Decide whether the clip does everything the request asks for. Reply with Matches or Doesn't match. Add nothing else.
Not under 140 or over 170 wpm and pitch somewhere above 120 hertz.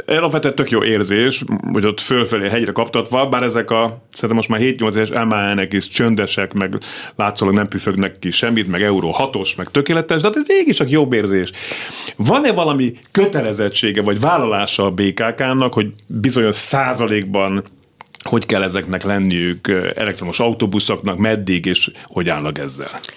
Doesn't match